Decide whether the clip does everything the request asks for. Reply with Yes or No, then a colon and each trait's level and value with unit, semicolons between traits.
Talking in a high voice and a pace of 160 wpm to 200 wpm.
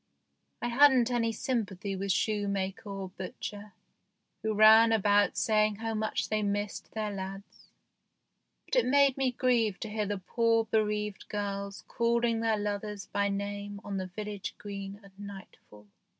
No: high, 210 Hz; average, 150 wpm